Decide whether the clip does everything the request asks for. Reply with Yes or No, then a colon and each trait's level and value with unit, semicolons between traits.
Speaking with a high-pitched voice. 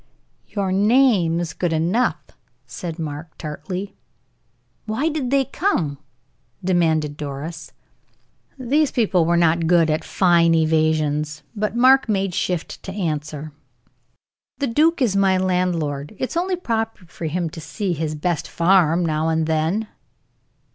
No: medium, 175 Hz